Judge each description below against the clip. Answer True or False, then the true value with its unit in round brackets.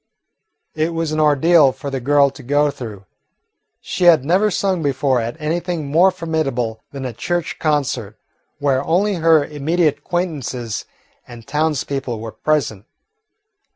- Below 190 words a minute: True (140 wpm)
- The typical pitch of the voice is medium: True (145 Hz)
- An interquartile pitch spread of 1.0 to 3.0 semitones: False (4.0 semitones)